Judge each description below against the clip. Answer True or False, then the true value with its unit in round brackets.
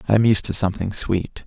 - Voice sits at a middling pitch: False (100 Hz)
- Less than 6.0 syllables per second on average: False (6.3 syllables/s)